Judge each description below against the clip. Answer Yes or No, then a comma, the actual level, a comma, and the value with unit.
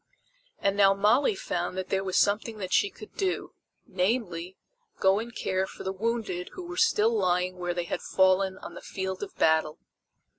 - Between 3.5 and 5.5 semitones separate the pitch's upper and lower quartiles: No, average, 2.7 semitones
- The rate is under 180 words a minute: No, average, 185 wpm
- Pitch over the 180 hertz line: Yes, high, 190 Hz